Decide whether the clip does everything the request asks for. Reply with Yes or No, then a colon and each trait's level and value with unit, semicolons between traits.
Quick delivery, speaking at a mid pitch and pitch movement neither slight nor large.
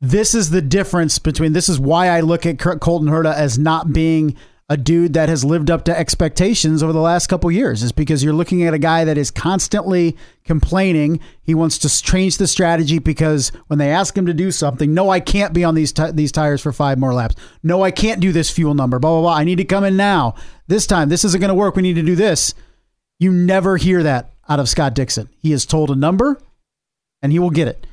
Yes: fast, 245 wpm; medium, 165 Hz; average, 3.2 semitones